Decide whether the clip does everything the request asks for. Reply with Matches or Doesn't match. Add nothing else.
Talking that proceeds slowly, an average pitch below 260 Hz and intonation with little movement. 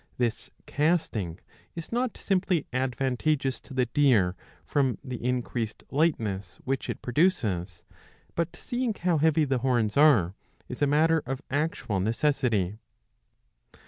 Doesn't match